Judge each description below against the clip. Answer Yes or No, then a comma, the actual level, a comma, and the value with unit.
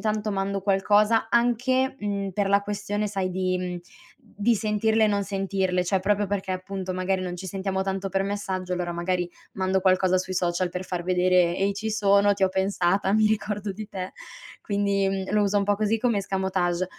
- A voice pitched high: Yes, high, 195 Hz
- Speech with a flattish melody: Yes, narrow, 1.8 semitones